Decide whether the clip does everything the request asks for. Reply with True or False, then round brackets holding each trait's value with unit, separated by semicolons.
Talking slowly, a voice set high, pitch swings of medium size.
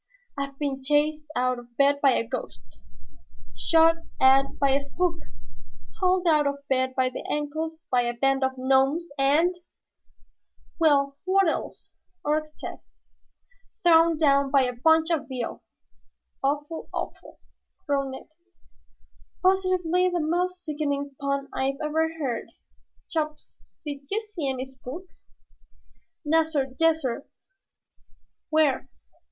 True (125 wpm; 290 Hz; 3.2 semitones)